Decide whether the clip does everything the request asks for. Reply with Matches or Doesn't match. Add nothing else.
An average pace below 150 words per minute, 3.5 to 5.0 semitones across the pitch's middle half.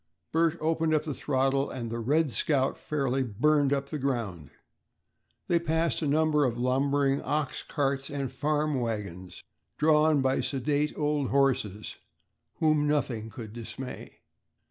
Doesn't match